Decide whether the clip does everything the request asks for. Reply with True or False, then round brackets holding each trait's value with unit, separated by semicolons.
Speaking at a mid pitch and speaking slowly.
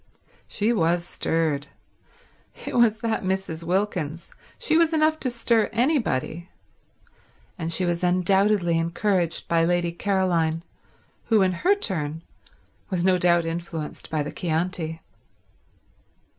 True (175 Hz; 120 wpm)